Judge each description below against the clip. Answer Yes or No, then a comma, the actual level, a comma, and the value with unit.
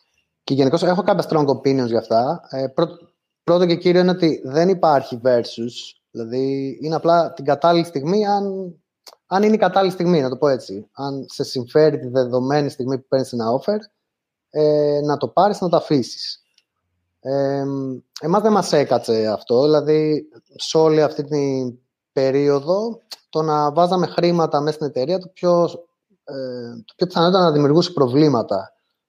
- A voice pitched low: No, medium, 150 Hz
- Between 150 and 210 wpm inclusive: Yes, average, 165 wpm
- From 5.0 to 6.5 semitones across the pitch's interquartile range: No, average, 4.5 semitones